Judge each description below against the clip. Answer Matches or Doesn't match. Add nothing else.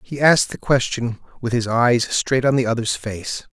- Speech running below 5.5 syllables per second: Matches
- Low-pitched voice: Matches